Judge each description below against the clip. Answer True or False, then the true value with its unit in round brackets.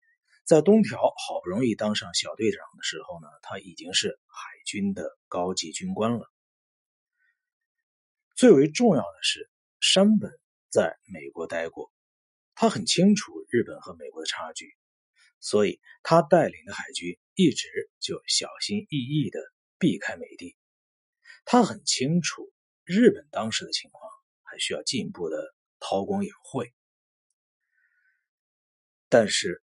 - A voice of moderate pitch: False (215 Hz)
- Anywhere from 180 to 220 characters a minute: True (195 characters per minute)